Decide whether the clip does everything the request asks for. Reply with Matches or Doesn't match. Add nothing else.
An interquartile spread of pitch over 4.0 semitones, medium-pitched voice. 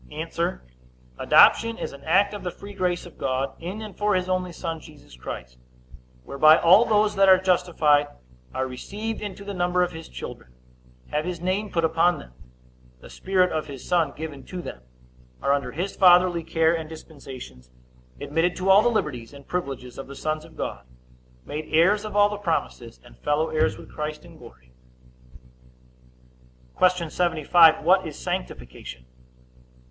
Matches